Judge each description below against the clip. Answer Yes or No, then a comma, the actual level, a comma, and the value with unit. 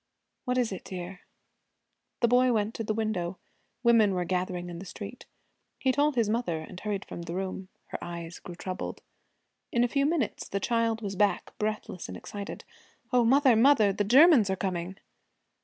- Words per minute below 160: No, average, 180 wpm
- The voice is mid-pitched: No, high, 205 Hz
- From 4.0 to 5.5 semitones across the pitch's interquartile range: Yes, average, 4.4 semitones